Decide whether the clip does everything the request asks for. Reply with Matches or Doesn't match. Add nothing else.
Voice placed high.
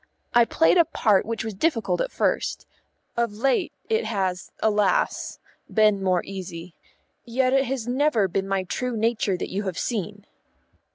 Matches